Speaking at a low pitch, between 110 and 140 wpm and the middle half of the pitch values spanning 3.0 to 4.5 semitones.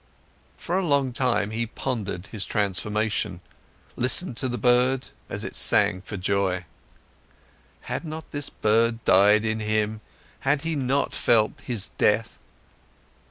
Yes: low, 115 Hz; slow, 135 wpm; average, 3.9 semitones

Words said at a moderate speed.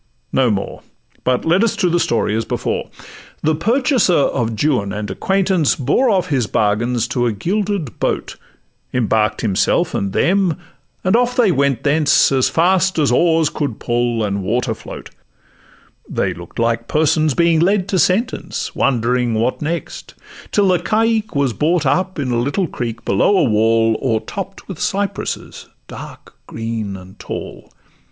Yes: average, 155 wpm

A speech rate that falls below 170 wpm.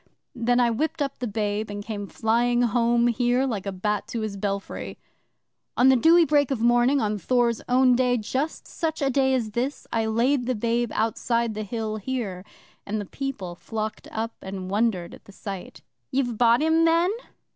No: average, 190 wpm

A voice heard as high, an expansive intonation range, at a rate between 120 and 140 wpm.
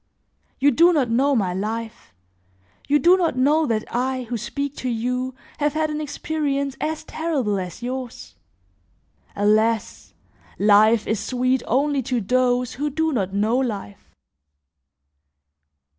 No: very high, 255 Hz; average, 4.4 semitones; slow, 135 wpm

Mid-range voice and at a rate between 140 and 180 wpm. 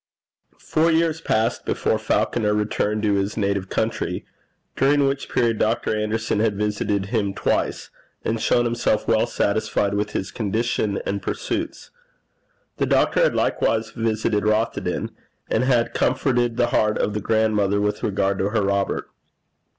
No: low, 110 Hz; average, 145 wpm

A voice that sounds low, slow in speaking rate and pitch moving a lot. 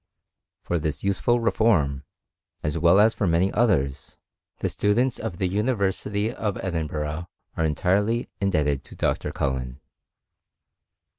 Yes: very low, 90 Hz; slow, 130 wpm; wide, 5.7 semitones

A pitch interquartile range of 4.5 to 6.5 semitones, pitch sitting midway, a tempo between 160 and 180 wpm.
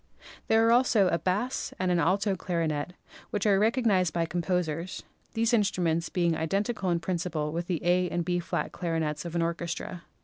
No: average, 2.8 semitones; medium, 180 Hz; average, 175 wpm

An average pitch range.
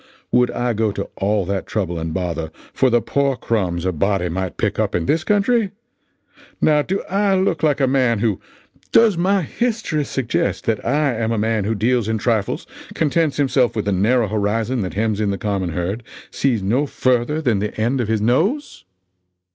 No: wide, 6.0 semitones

